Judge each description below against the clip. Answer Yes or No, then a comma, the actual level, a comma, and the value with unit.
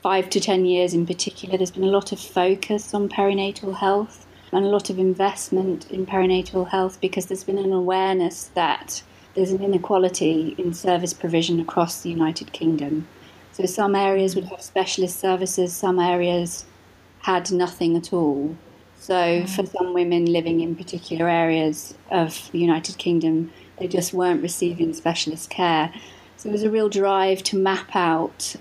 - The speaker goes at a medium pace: Yes, average, 165 wpm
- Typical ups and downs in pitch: No, narrow, 2.2 semitones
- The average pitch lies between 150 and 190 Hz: Yes, medium, 185 Hz